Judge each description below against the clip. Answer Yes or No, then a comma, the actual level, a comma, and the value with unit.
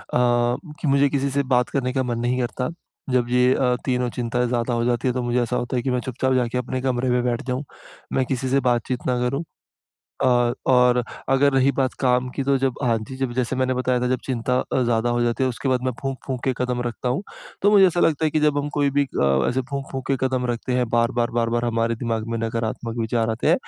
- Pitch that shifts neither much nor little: No, narrow, 1.7 semitones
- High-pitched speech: No, low, 125 Hz